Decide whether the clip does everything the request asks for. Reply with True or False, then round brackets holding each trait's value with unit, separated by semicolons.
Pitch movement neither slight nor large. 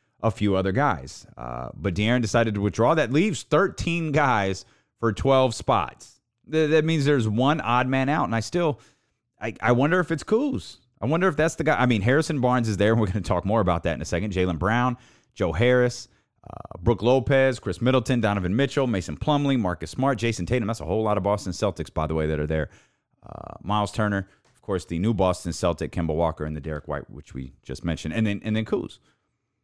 False (6.0 semitones)